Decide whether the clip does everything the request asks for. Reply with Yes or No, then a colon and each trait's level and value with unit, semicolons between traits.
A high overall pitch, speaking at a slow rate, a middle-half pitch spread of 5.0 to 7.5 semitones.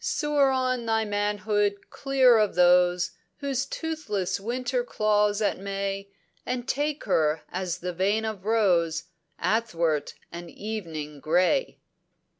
Yes: high, 205 Hz; slow, 120 wpm; wide, 5.6 semitones